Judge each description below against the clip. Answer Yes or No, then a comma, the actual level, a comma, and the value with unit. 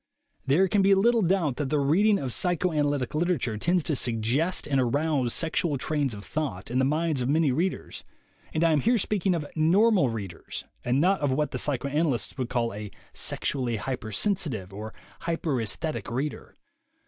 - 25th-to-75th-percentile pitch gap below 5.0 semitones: No, wide, 5.5 semitones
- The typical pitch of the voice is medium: Yes, medium, 145 Hz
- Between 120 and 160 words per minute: No, average, 170 wpm